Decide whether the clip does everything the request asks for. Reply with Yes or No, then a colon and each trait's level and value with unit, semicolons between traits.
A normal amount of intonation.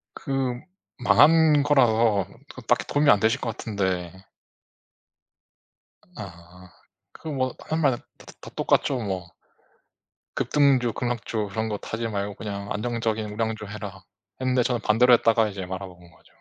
Yes: average, 4.0 semitones